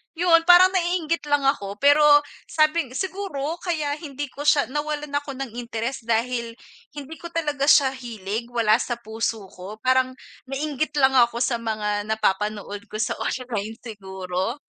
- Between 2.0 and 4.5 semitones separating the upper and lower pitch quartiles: No, average, 5.2 semitones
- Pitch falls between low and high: No, very high, 260 Hz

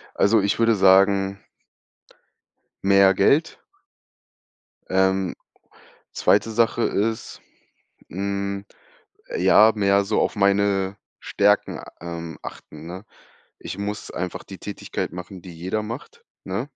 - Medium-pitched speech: No, low, 100 Hz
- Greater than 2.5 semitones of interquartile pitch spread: No, narrow, 1.7 semitones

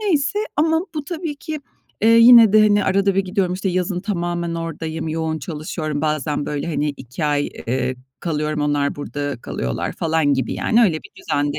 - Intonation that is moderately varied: No, wide, 5.7 semitones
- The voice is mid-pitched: Yes, medium, 165 Hz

